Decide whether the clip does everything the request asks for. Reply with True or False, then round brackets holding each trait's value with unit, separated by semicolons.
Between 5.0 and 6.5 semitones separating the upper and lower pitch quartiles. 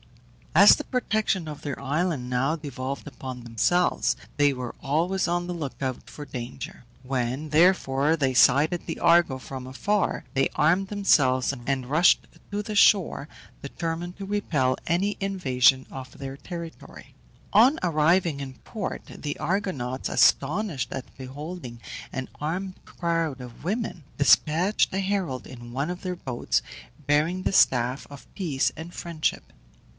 True (5.3 semitones)